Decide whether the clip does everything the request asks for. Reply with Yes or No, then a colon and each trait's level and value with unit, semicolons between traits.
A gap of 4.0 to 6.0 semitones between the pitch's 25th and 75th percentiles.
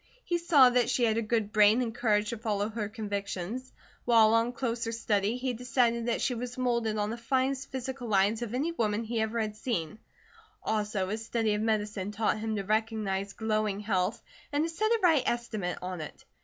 No: narrow, 2.6 semitones